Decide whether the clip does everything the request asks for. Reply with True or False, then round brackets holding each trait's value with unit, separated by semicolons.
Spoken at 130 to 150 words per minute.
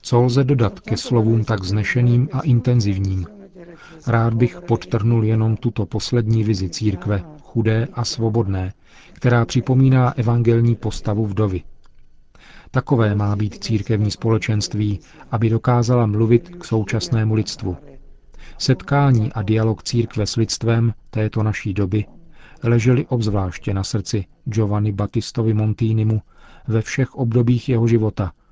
False (120 wpm)